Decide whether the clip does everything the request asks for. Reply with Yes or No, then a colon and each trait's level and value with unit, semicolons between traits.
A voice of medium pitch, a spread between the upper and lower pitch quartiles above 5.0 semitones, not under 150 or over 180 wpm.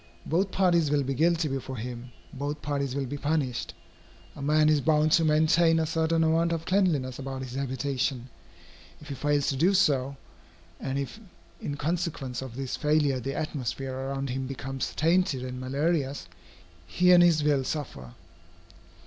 No: medium, 145 Hz; average, 3.2 semitones; average, 165 wpm